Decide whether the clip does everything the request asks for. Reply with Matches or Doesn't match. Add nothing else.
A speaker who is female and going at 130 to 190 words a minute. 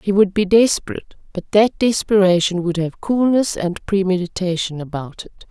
Matches